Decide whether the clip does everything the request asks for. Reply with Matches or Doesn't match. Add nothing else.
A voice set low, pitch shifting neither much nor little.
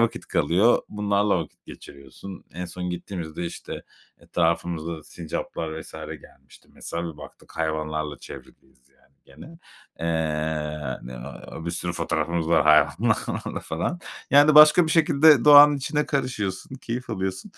Doesn't match